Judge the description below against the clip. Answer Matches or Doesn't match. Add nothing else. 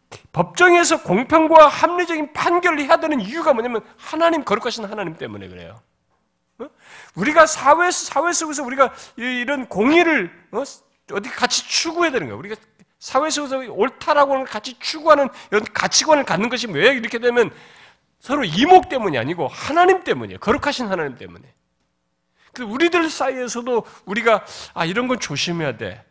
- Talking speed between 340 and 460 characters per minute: Matches